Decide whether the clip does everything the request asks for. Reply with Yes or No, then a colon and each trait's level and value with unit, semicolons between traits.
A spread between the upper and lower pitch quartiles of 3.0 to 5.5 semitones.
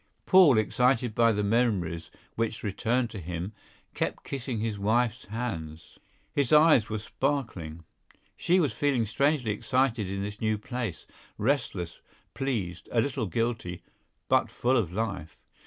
Yes: average, 4.1 semitones